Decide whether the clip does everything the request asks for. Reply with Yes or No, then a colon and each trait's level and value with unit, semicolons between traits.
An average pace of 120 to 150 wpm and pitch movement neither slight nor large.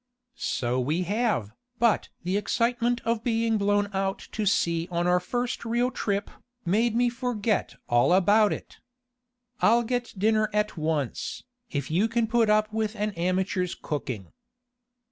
Yes: average, 145 wpm; average, 4.5 semitones